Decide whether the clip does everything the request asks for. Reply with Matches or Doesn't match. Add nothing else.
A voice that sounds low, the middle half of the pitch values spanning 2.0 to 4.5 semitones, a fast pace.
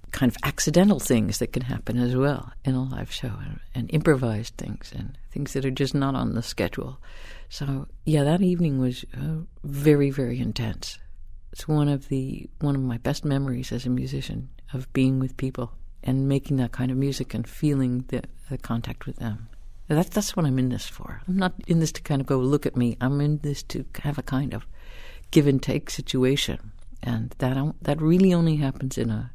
Matches